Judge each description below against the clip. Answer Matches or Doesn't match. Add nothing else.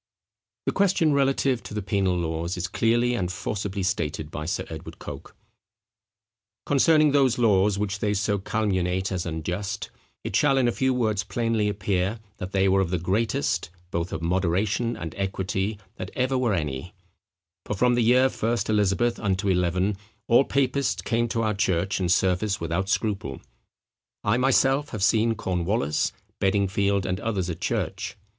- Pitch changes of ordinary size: Matches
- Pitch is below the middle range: Matches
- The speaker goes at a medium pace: Matches